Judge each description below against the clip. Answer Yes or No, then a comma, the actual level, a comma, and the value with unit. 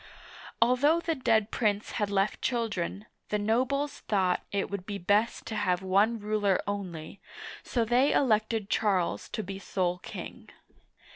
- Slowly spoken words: No, average, 150 wpm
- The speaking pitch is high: Yes, high, 210 Hz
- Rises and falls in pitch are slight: No, average, 3.0 semitones